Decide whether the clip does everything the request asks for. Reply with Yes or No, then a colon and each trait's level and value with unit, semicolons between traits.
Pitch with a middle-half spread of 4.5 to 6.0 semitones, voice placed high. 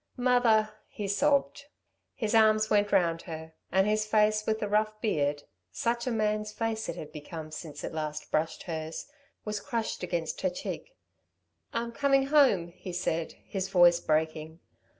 Yes: average, 5.0 semitones; high, 205 Hz